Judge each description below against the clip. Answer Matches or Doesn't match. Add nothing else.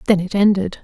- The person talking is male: Doesn't match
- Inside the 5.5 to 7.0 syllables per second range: Matches